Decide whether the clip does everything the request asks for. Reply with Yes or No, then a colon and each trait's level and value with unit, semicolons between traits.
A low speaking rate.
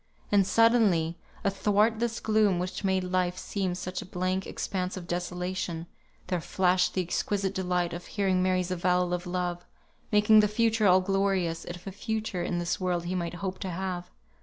No: average, 175 wpm